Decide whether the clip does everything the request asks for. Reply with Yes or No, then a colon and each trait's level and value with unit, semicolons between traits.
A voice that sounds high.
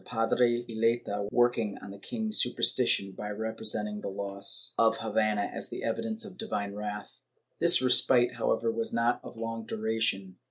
No: low, 115 Hz